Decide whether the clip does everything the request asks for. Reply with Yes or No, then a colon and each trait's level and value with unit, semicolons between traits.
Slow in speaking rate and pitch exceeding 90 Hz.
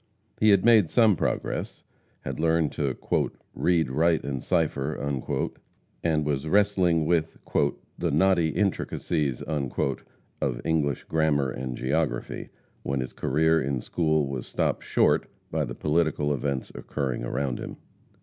No: slow, 130 wpm; very low, 75 Hz